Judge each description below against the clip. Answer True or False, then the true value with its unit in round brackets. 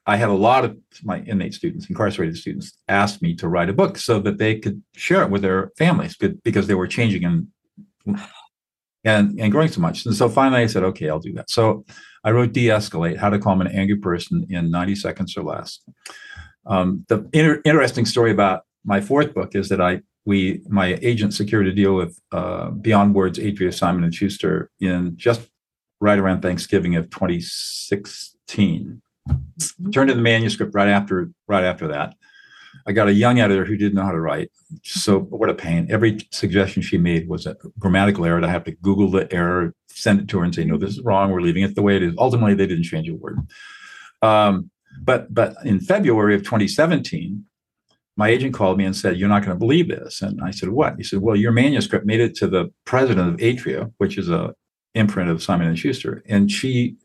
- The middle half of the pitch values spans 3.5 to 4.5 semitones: True (3.9 semitones)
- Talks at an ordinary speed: False (210 wpm)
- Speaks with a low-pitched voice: True (100 Hz)